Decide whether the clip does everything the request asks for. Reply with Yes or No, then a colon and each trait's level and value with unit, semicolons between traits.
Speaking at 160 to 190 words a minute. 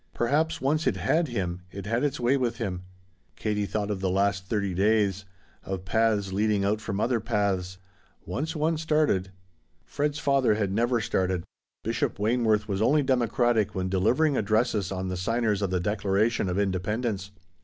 Yes: average, 165 wpm